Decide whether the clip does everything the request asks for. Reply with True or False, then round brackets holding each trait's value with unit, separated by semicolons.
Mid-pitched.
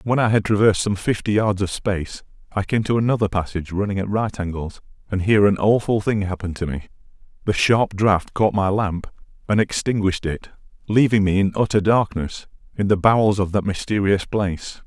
False (100 Hz)